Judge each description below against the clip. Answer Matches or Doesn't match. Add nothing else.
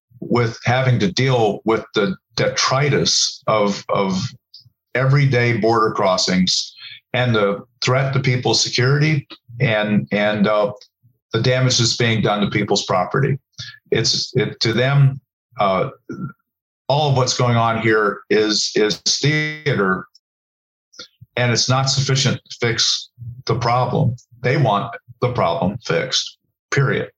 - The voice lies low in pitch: Matches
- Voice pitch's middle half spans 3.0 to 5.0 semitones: Doesn't match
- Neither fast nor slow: Doesn't match